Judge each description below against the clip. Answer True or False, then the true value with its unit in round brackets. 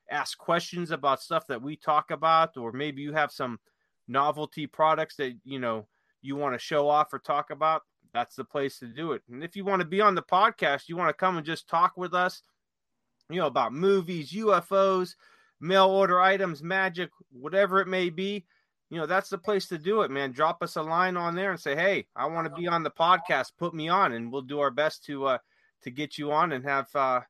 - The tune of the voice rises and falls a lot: False (4.4 semitones)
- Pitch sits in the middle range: True (160 Hz)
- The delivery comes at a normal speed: False (230 wpm)